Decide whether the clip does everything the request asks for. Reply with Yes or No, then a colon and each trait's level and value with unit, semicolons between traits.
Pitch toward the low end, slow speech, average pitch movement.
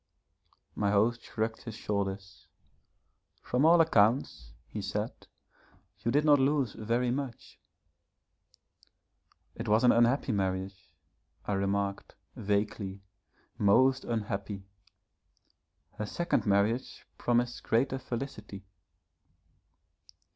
Yes: low, 110 Hz; slow, 95 wpm; average, 3.7 semitones